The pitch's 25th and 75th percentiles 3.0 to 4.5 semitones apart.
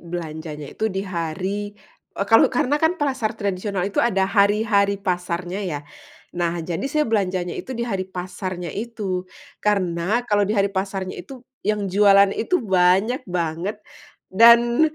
Yes: average, 3.4 semitones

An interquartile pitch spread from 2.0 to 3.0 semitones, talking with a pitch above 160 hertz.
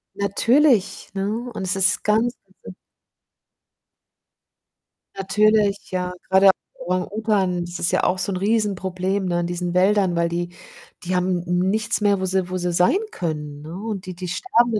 Yes: narrow, 2.6 semitones; medium, 185 Hz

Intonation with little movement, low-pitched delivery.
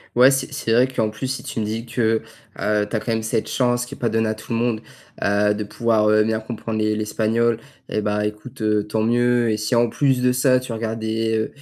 Yes: narrow, 2.1 semitones; low, 110 Hz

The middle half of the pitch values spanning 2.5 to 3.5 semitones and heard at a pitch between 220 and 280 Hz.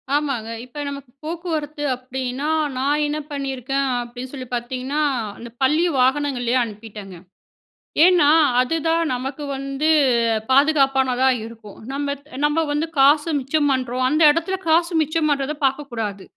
Yes: average, 2.9 semitones; very high, 275 Hz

